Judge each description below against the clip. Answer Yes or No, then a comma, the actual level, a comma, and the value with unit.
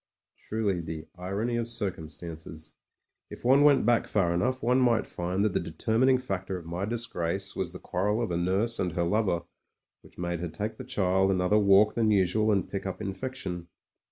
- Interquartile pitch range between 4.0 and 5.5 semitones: Yes, average, 4.3 semitones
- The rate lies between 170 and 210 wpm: Yes, average, 185 wpm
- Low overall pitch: Yes, very low, 95 Hz